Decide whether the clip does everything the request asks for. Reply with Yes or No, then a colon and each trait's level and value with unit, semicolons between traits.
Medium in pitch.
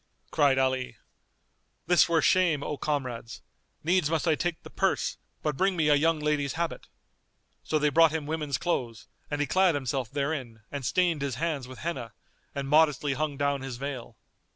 Yes: medium, 145 Hz